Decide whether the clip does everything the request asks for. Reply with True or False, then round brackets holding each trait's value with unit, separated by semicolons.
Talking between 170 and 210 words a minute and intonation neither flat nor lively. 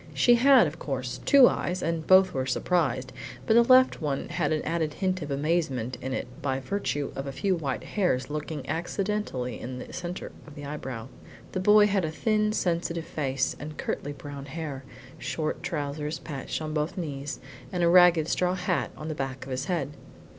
True (190 wpm; 4.7 semitones)